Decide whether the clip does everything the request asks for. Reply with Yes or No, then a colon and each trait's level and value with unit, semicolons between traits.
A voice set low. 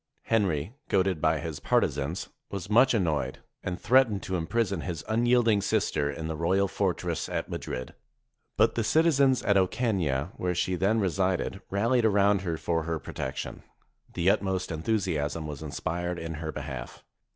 Yes: very low, 95 Hz